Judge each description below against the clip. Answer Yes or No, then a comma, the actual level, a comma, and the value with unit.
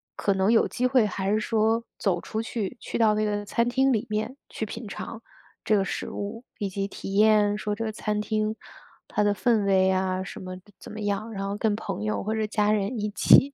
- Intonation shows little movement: Yes, narrow, 1.9 semitones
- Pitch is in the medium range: No, high, 210 Hz